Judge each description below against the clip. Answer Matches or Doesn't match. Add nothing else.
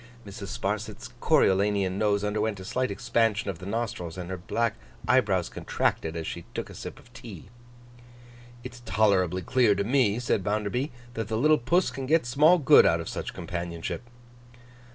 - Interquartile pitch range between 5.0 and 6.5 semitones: Doesn't match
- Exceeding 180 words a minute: Doesn't match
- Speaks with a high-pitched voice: Doesn't match